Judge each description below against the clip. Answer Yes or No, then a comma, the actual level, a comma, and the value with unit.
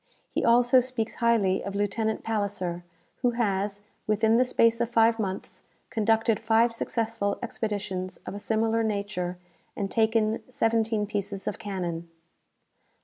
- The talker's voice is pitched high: Yes, high, 220 Hz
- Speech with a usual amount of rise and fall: No, narrow, 2.2 semitones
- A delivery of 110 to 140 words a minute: Yes, slow, 135 wpm